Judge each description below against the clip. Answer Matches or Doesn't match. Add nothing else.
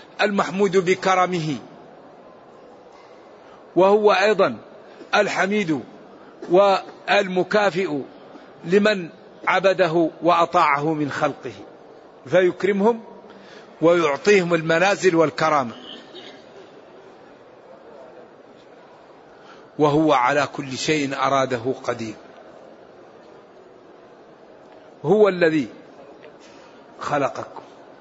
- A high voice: Doesn't match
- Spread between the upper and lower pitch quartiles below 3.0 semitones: Doesn't match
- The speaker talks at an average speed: Doesn't match